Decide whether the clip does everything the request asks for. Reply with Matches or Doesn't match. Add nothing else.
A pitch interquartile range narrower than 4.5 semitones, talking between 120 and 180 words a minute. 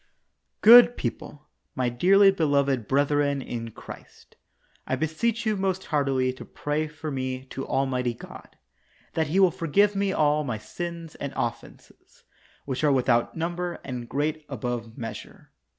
Doesn't match